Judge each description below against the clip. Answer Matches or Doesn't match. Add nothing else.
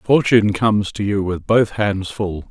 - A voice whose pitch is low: Matches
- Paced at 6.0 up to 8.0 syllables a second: Doesn't match